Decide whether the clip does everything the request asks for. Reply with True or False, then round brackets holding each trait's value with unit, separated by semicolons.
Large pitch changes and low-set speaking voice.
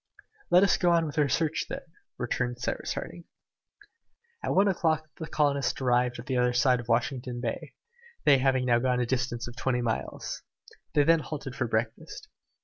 False (3.6 semitones; 130 Hz)